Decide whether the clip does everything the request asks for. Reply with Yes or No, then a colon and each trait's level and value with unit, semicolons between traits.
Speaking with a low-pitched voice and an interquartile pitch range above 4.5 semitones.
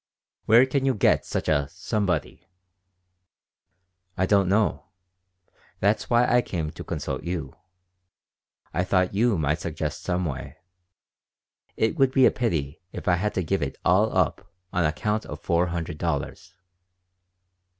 Yes: very low, 90 Hz; average, 4.9 semitones